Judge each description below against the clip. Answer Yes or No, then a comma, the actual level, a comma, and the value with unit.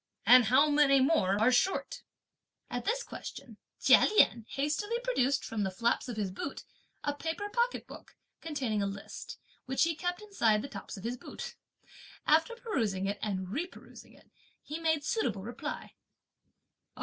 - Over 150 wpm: Yes, average, 160 wpm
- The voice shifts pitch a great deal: Yes, wide, 7.4 semitones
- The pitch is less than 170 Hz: No, very high, 275 Hz